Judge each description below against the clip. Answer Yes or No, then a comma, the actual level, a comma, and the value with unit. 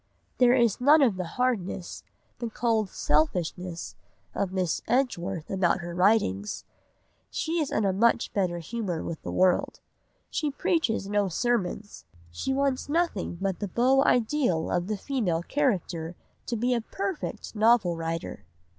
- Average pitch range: No, wide, 5.9 semitones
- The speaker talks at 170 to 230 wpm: No, average, 145 wpm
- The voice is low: No, high, 205 Hz